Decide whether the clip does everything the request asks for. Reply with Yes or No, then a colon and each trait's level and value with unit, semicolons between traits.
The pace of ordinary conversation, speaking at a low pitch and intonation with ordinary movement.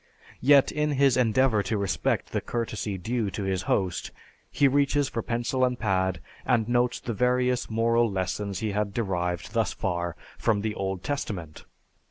Yes: average, 165 wpm; low, 110 Hz; average, 4.5 semitones